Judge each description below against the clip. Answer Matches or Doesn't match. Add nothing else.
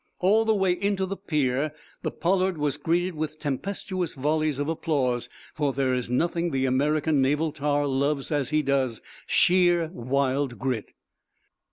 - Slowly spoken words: Doesn't match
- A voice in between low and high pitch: Matches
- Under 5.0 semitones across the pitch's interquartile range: Matches